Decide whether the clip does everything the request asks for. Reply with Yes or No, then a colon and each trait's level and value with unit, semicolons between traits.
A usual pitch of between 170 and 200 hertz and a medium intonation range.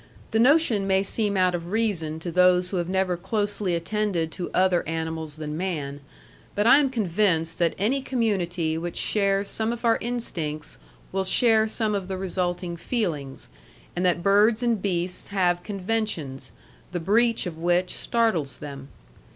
Yes: medium, 185 Hz; average, 4.1 semitones